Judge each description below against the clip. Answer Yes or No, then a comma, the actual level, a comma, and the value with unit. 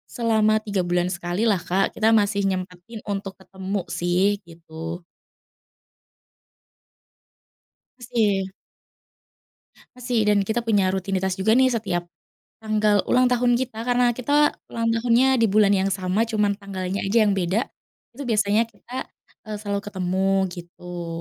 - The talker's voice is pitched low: No, high, 205 Hz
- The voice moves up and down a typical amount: Yes, average, 3.4 semitones